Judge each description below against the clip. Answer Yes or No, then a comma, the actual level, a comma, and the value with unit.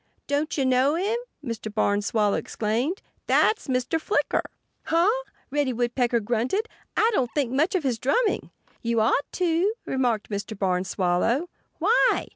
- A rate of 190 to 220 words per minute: No, average, 145 wpm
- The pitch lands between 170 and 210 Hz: No, very high, 255 Hz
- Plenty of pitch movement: Yes, wide, 6.6 semitones